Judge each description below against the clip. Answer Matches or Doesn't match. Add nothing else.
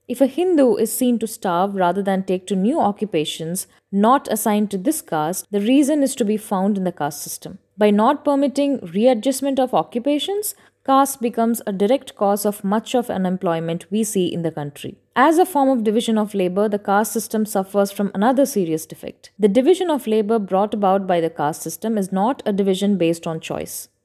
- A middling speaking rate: Doesn't match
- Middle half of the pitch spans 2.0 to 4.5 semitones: Doesn't match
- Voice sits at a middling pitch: Doesn't match